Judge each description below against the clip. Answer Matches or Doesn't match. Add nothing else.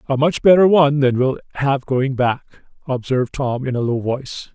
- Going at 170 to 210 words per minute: Matches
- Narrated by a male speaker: Matches